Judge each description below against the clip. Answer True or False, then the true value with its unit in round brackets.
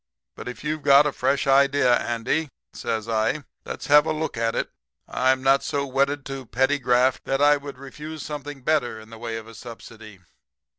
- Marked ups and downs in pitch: False (3.5 semitones)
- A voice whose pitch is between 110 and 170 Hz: True (135 Hz)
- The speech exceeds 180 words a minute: True (195 wpm)